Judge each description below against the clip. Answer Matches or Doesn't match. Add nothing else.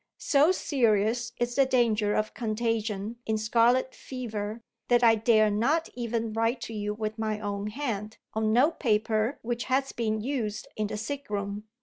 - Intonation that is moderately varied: Doesn't match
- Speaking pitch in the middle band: Doesn't match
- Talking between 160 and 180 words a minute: Matches